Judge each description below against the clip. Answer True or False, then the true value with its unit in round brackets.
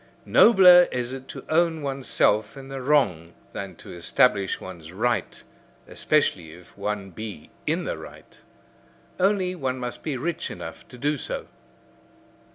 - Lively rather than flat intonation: True (7.4 semitones)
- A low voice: True (125 Hz)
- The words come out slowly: False (145 wpm)